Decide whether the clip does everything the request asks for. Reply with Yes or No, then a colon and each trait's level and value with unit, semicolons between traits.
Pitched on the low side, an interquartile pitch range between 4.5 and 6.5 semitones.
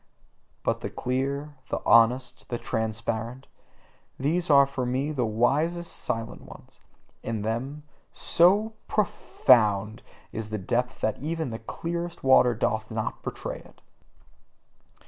Yes: low, 125 Hz; average, 5.0 semitones